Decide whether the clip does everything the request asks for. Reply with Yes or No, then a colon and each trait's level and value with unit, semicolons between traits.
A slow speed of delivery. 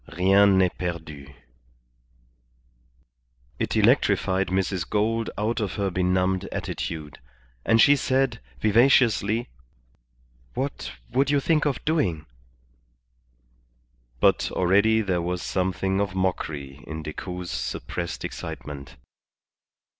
Yes: slow, 100 wpm